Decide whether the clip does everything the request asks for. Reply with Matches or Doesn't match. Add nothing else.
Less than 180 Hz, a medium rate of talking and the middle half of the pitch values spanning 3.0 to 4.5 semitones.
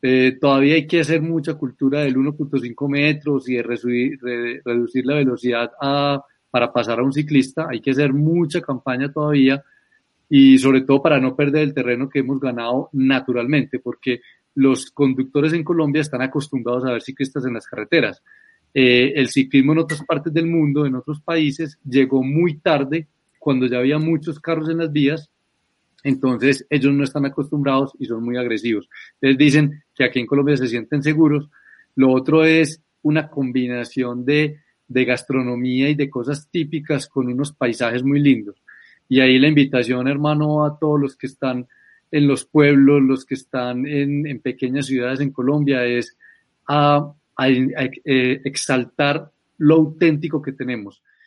Doesn't match